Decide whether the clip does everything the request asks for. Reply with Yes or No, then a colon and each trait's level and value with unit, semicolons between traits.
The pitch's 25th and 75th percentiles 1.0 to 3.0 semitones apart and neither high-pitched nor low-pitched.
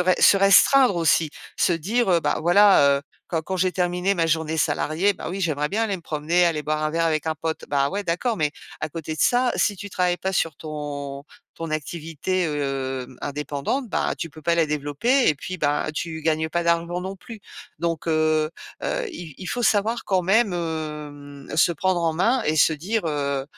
No: average, 3.6 semitones; medium, 165 Hz